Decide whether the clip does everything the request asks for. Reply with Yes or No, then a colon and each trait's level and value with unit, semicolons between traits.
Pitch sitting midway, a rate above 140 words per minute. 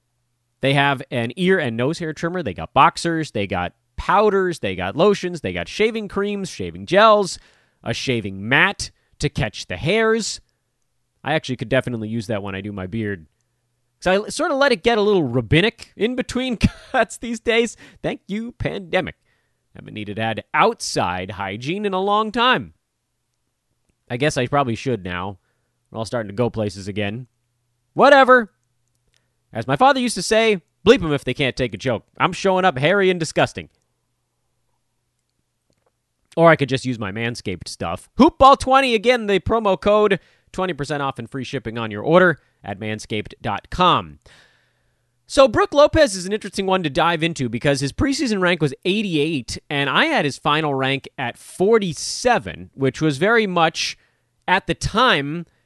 Yes: medium, 145 Hz; average, 170 wpm